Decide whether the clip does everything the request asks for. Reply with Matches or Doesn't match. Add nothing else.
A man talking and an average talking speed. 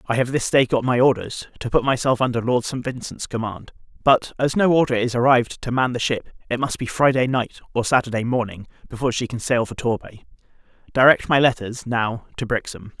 Doesn't match